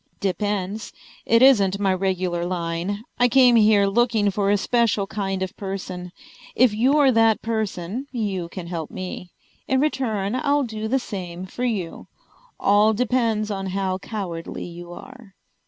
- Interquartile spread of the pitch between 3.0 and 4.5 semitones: Yes, average, 3.7 semitones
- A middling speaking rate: Yes, average, 150 wpm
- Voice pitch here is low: No, high, 205 Hz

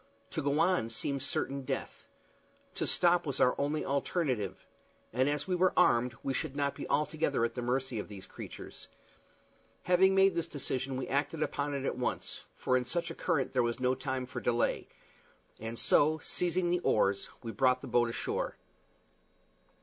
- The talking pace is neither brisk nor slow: Yes, average, 180 wpm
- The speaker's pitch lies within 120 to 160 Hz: Yes, low, 135 Hz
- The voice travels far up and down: No, average, 4.0 semitones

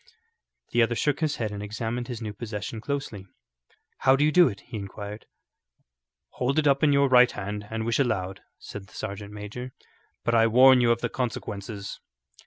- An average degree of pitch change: Yes, average, 3.9 semitones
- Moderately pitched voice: No, low, 115 Hz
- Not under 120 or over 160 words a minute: No, average, 190 wpm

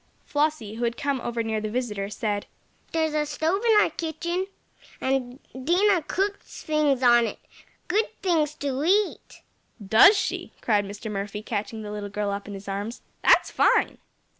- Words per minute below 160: No, average, 165 wpm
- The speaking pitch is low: No, very high, 255 Hz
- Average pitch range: No, wide, 7.1 semitones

